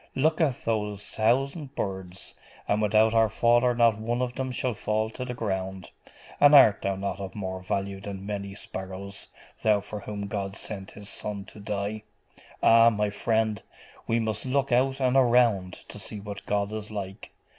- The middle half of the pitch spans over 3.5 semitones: No, average, 3.1 semitones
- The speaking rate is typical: Yes, average, 175 wpm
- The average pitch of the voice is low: Yes, low, 105 Hz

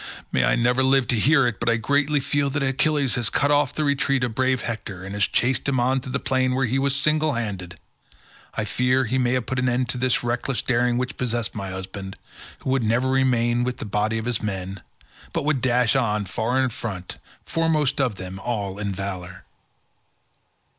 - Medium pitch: No, low, 125 Hz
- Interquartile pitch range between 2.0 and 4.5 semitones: Yes, average, 3.7 semitones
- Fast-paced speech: Yes, fast, 210 wpm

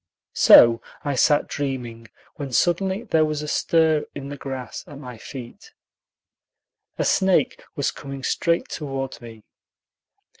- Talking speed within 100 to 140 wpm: Yes, slow, 135 wpm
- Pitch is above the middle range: No, medium, 140 Hz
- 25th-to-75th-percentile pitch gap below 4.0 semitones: Yes, average, 3.6 semitones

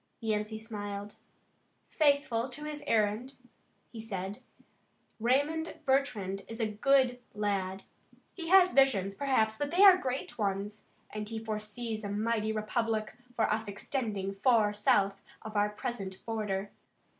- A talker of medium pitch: No, high, 220 Hz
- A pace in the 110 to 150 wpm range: Yes, slow, 135 wpm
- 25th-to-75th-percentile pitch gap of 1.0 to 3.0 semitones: No, average, 3.7 semitones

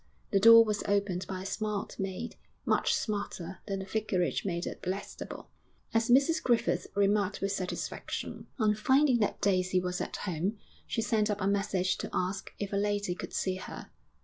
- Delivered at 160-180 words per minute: Yes, average, 175 wpm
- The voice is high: Yes, high, 200 Hz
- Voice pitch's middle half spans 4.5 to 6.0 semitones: No, narrow, 2.4 semitones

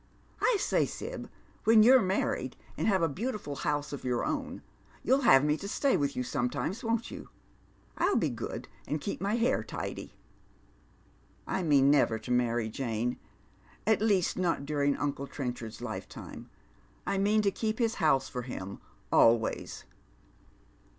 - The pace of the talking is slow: No, average, 160 wpm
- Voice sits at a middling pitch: Yes, medium, 150 Hz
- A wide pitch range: Yes, wide, 8.7 semitones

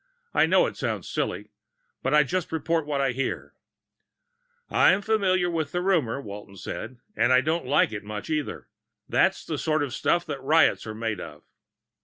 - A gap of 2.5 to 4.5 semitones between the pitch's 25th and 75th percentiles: No, wide, 5.6 semitones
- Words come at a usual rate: Yes, average, 175 wpm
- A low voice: No, medium, 150 Hz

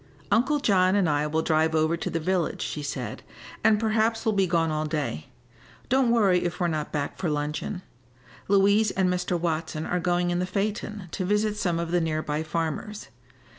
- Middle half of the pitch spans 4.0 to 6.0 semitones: Yes, average, 4.3 semitones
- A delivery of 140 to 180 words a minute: No, average, 195 wpm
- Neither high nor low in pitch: Yes, medium, 175 Hz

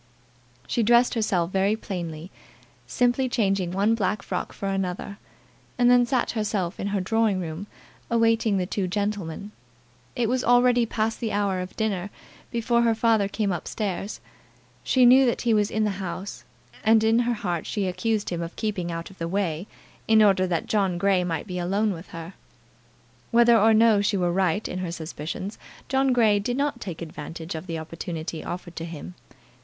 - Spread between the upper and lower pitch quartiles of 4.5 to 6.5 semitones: No, average, 4.0 semitones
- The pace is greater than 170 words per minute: Yes, average, 180 wpm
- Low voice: No, high, 200 Hz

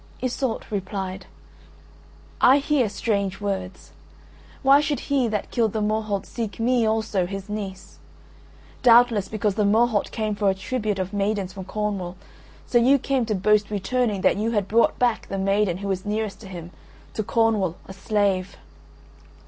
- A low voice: No, high, 210 Hz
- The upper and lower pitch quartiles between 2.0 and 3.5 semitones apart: Yes, average, 2.9 semitones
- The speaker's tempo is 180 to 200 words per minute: No, average, 160 wpm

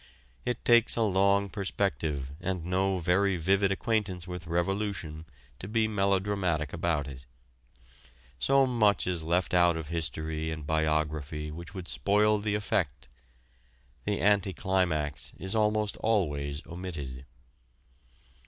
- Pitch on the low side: Yes, very low, 90 Hz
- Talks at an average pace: No, slow, 125 wpm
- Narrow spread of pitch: No, average, 4.4 semitones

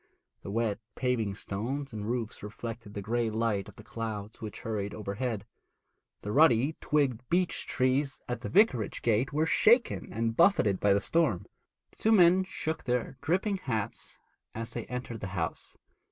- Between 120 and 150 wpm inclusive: No, average, 165 wpm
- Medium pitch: No, low, 115 Hz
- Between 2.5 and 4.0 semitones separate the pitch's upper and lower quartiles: No, average, 5.0 semitones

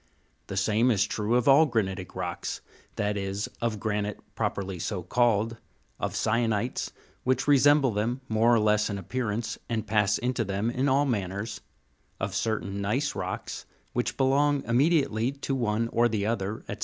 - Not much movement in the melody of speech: No, average, 3.5 semitones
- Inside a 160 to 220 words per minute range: Yes, average, 165 wpm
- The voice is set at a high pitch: No, low, 110 Hz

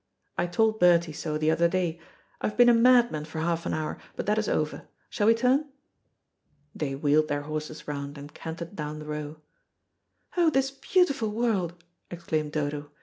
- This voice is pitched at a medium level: Yes, medium, 170 Hz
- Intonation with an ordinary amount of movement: No, wide, 6.4 semitones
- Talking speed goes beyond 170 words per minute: Yes, average, 180 wpm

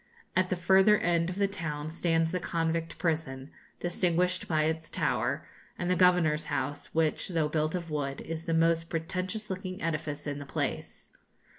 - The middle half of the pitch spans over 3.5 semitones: No, average, 2.7 semitones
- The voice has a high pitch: No, medium, 165 Hz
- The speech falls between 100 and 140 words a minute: No, average, 170 wpm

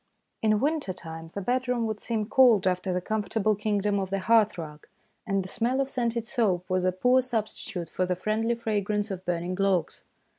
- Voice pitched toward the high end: Yes, high, 210 Hz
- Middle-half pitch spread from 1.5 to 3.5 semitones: No, average, 3.9 semitones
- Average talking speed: Yes, average, 190 wpm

